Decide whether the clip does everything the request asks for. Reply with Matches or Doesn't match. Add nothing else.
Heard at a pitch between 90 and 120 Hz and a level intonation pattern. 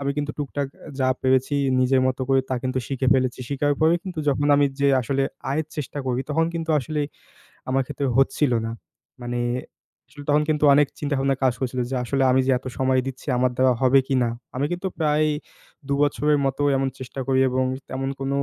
Doesn't match